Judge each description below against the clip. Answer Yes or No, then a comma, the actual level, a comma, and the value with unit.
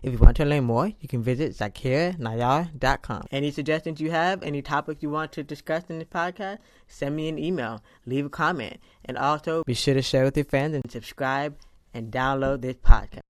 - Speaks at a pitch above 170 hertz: No, medium, 140 Hz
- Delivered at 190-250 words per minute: Yes, fast, 205 wpm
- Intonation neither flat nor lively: Yes, average, 3.6 semitones